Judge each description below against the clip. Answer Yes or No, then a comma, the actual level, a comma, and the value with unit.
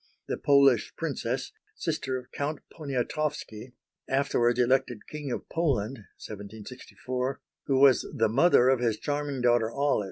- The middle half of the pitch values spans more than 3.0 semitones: No, average, 2.7 semitones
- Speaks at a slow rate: Yes, slow, 130 wpm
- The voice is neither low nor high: No, low, 130 Hz